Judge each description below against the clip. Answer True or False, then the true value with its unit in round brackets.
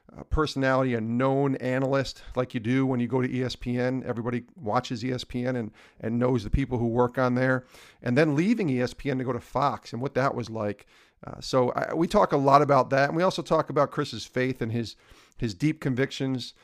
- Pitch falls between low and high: False (130 Hz)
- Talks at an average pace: False (215 wpm)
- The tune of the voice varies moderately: False (2.1 semitones)